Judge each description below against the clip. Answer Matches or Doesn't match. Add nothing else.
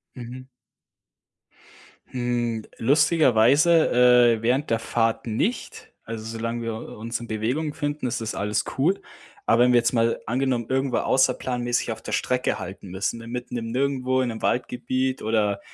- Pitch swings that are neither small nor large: Doesn't match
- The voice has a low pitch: Matches